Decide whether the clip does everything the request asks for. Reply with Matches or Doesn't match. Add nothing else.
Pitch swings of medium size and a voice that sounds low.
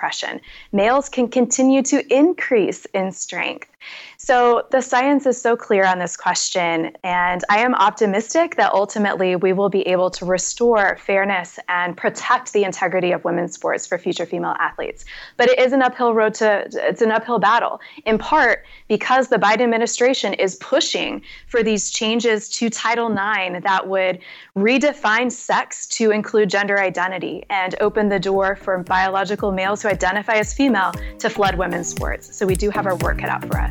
Doesn't match